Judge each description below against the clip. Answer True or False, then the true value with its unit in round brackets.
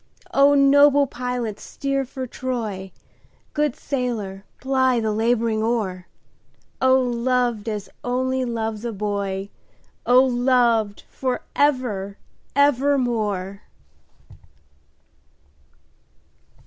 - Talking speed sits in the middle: False (75 wpm)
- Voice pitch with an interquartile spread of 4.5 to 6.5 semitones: False (3.5 semitones)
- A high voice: True (245 Hz)